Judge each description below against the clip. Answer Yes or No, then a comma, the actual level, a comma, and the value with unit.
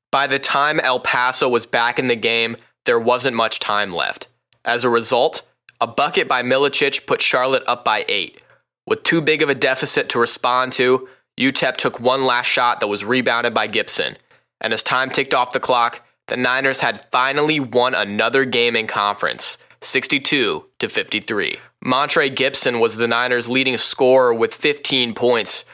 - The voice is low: Yes, low, 125 Hz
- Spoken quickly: No, average, 175 wpm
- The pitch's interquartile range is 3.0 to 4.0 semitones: No, narrow, 2.5 semitones